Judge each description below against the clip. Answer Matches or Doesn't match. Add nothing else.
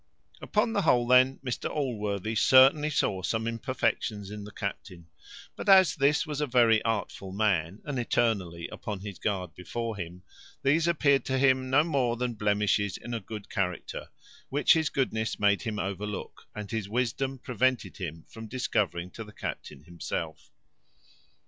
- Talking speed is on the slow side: Doesn't match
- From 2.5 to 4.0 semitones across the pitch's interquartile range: Doesn't match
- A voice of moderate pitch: Doesn't match